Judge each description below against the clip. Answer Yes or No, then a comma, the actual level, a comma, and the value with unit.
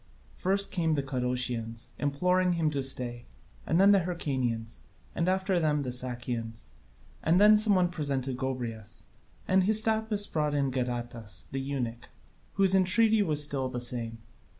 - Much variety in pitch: Yes, wide, 6.9 semitones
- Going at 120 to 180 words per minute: Yes, average, 150 wpm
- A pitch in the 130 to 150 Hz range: Yes, medium, 140 Hz